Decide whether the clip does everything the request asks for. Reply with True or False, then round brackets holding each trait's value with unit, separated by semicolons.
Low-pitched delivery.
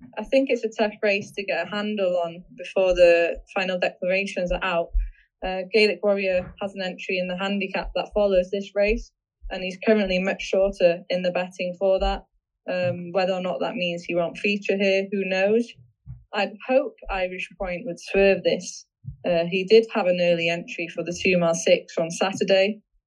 False (190 Hz)